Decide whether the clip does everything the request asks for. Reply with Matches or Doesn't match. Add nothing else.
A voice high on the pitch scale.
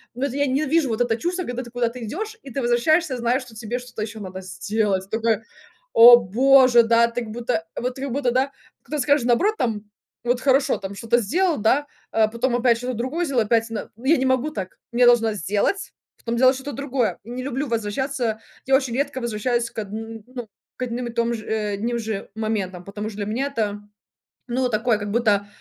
Matches